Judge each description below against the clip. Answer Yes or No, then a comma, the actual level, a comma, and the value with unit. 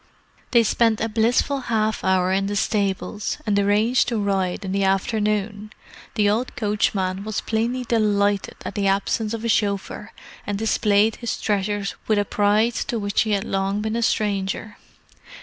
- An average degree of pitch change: No, narrow, 1.9 semitones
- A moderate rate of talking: Yes, average, 165 wpm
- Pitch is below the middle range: No, high, 210 Hz